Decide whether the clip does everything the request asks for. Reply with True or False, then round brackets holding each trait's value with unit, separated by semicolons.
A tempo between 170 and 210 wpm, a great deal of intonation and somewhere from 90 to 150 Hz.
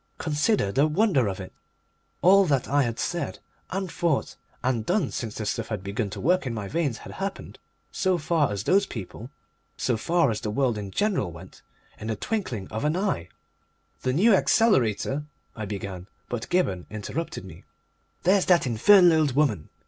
True (180 wpm; 8.6 semitones; 135 Hz)